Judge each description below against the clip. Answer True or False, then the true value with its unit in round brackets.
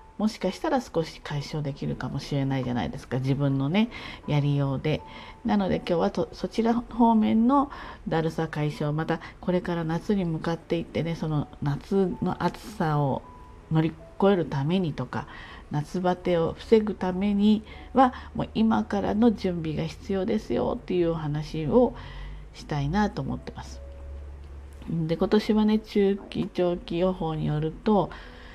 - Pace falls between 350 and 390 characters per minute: False (295 characters per minute)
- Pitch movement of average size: False (6.2 semitones)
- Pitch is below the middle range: False (170 Hz)